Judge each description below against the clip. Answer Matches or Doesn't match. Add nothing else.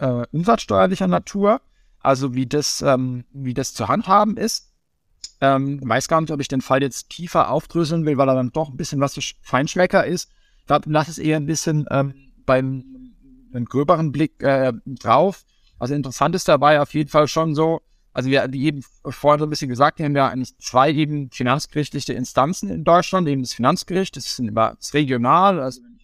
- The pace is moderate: Doesn't match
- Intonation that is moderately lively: Matches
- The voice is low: Doesn't match